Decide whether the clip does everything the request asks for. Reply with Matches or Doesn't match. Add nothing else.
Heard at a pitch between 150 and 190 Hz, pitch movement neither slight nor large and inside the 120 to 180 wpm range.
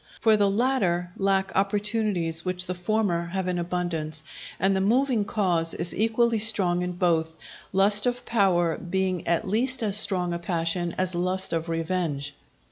Matches